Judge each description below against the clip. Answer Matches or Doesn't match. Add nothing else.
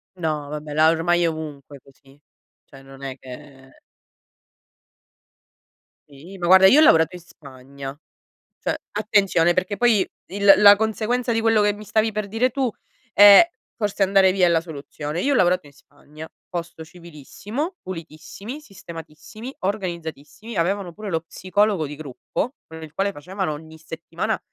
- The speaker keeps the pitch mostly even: Doesn't match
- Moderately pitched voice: Matches